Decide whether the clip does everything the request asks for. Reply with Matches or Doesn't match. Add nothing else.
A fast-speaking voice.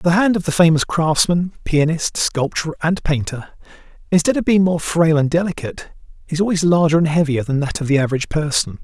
Doesn't match